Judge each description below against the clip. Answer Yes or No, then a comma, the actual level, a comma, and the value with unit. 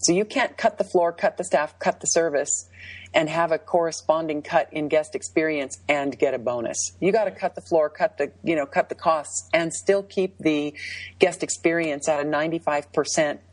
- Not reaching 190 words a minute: No, average, 200 wpm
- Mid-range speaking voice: Yes, medium, 155 Hz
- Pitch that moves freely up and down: No, average, 3.1 semitones